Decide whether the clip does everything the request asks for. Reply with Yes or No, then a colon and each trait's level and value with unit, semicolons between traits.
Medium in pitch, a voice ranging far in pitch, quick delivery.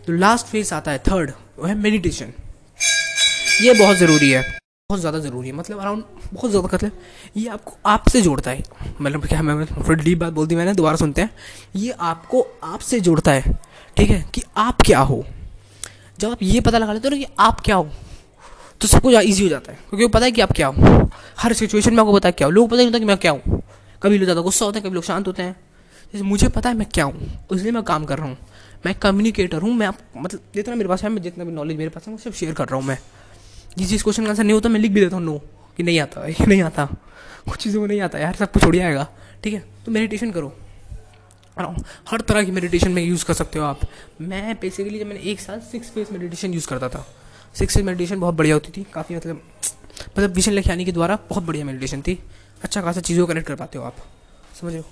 Yes: medium, 180 Hz; wide, 6.1 semitones; fast, 250 wpm